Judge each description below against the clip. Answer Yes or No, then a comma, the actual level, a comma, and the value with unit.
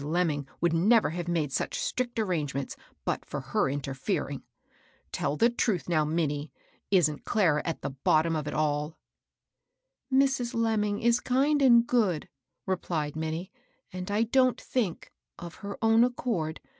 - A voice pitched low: No, medium, 175 Hz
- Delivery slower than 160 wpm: Yes, average, 150 wpm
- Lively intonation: Yes, wide, 7.0 semitones